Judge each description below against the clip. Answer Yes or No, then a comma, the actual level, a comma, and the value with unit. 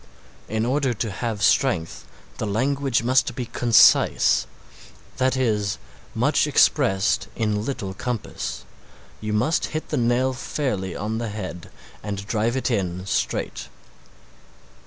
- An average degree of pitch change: Yes, average, 4.0 semitones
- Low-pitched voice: Yes, low, 115 Hz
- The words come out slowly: Yes, slow, 125 wpm